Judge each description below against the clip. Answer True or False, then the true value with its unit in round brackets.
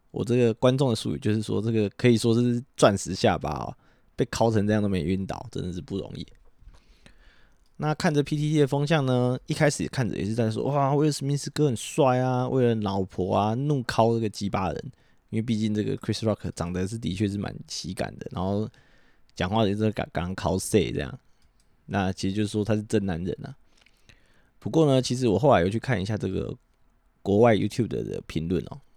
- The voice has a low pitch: True (110 Hz)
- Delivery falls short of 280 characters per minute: False (330 characters per minute)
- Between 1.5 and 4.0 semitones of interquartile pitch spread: False (4.6 semitones)